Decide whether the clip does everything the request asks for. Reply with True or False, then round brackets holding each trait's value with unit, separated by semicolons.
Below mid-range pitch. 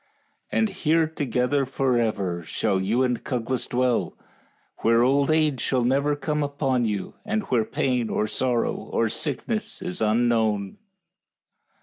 True (125 Hz)